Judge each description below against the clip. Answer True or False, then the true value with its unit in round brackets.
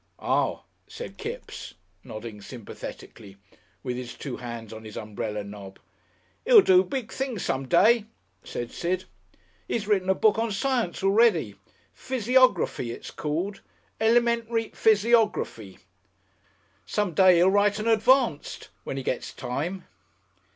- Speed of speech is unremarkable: False (125 wpm)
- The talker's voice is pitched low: False (190 Hz)